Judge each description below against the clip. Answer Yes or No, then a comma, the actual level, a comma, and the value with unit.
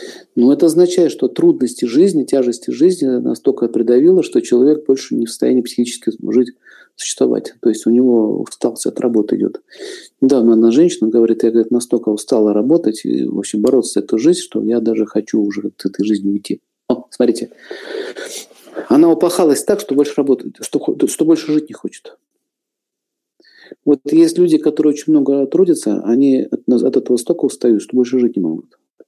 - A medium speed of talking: No, fast, 170 wpm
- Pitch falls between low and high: Yes, medium, 150 Hz